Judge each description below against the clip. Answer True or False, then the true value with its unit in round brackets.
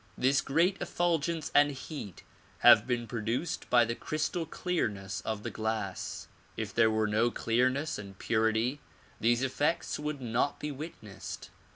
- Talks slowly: False (145 wpm)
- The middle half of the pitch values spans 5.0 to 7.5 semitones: True (5.3 semitones)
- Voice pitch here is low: True (125 Hz)